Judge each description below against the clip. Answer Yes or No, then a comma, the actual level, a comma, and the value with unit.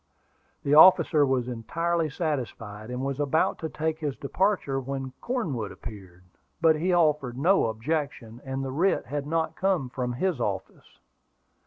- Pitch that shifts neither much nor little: Yes, average, 4.6 semitones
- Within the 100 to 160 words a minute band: Yes, average, 150 wpm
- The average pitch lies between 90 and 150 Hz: Yes, medium, 140 Hz